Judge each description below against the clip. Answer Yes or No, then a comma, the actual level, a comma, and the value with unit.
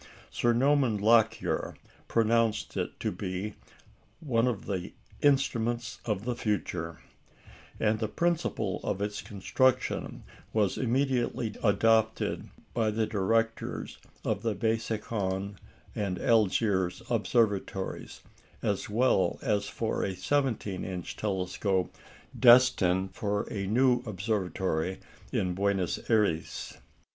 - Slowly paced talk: Yes, slow, 105 wpm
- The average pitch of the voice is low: Yes, low, 110 Hz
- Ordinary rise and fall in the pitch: Yes, average, 3.3 semitones